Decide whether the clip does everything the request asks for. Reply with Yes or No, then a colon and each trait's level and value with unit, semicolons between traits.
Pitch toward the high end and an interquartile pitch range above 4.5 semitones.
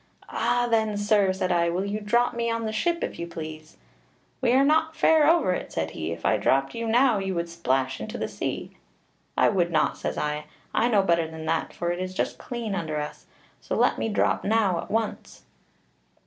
Yes: high, 195 Hz; wide, 5.6 semitones